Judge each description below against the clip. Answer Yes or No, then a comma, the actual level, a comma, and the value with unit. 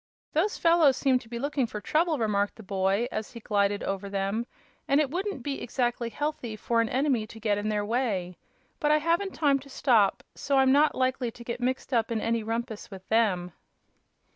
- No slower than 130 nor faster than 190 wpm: No, fast, 205 wpm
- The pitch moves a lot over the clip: No, average, 4.7 semitones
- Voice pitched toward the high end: Yes, high, 235 Hz